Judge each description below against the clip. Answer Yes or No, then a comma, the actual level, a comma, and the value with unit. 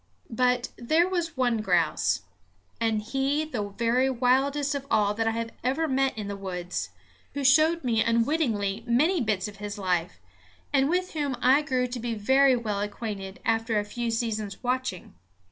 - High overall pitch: Yes, high, 235 Hz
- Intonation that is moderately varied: Yes, average, 4.5 semitones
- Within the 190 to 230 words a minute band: No, average, 170 wpm